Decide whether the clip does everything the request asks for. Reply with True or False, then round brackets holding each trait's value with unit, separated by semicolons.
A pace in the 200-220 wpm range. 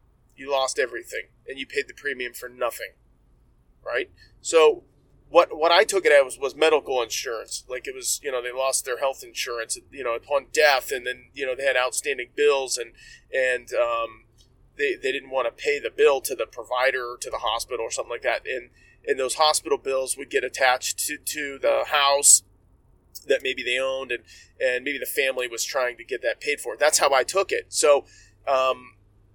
True (205 wpm)